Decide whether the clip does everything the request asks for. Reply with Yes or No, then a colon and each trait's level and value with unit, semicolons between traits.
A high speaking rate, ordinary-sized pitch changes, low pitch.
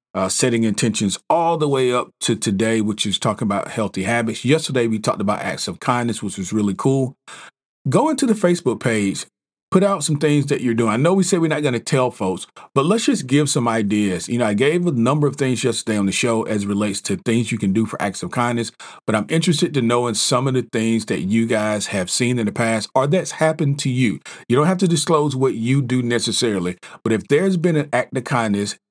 Yes: fast, 245 wpm; average, 5.0 semitones; low, 120 Hz